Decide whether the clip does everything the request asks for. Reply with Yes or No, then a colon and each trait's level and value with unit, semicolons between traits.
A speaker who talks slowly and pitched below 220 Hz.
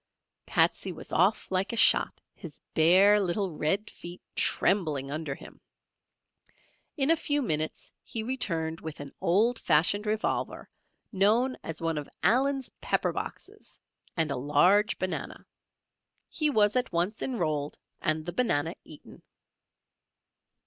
Yes: slow, 130 wpm; medium, 185 Hz